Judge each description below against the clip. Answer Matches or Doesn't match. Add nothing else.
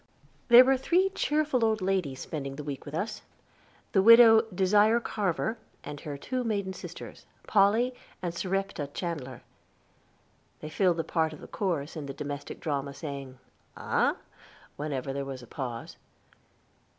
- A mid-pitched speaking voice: Matches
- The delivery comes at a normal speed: Matches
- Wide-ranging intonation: Matches